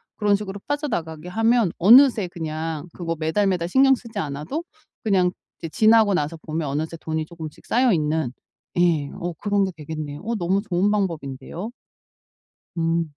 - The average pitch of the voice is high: No, medium, 175 Hz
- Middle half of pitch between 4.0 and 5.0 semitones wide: Yes, average, 4.7 semitones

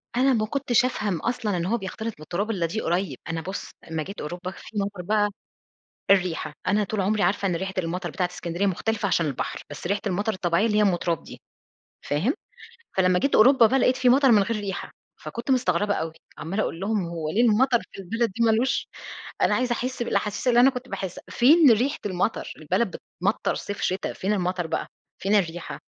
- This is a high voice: Yes, high, 200 Hz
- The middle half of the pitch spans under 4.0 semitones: No, average, 4.4 semitones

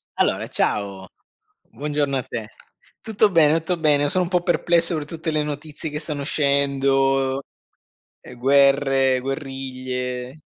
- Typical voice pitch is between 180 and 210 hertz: No, medium, 140 Hz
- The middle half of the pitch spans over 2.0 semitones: Yes, narrow, 2.5 semitones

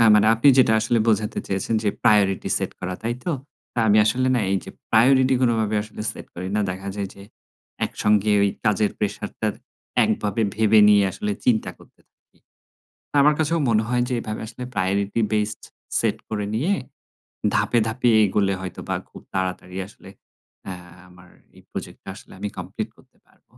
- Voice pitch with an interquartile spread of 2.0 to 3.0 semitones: Yes, narrow, 2.5 semitones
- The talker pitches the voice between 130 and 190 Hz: No, low, 105 Hz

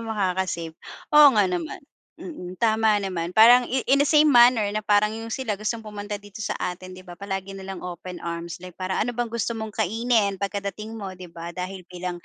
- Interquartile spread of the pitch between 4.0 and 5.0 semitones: No, average, 3.5 semitones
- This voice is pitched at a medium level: No, high, 200 Hz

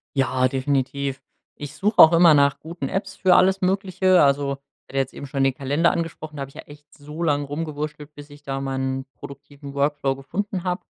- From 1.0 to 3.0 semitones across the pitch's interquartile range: No, average, 3.5 semitones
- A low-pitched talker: No, medium, 145 Hz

